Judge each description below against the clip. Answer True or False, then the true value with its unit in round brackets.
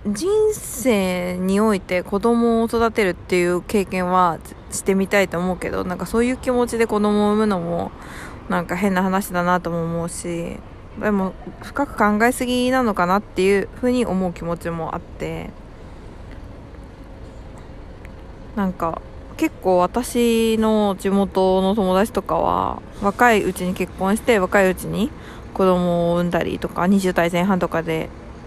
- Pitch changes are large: False (3.5 semitones)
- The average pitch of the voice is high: True (195 Hz)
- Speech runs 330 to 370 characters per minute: False (280 characters per minute)